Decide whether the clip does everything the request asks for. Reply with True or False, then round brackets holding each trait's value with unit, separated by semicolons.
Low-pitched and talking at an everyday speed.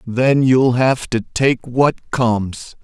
True (125 Hz; 150 wpm)